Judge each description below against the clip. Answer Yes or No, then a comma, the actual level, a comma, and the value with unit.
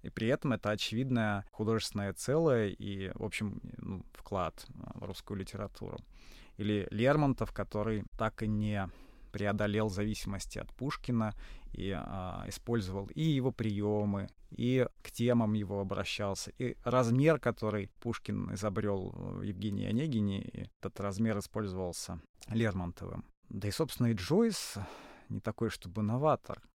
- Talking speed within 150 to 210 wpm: No, average, 130 wpm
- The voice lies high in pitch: No, low, 105 Hz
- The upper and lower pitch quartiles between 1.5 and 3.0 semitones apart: Yes, average, 2.7 semitones